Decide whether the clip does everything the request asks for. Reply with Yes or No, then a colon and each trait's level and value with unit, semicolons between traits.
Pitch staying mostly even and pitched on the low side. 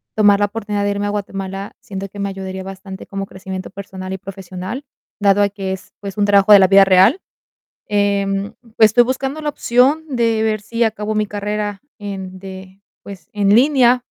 No: narrow, 1.8 semitones; high, 200 Hz